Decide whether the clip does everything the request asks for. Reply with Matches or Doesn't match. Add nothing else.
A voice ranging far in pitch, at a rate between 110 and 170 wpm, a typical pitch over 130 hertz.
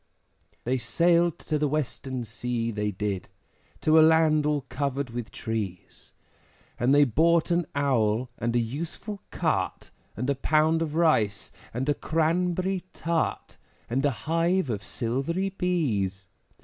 Matches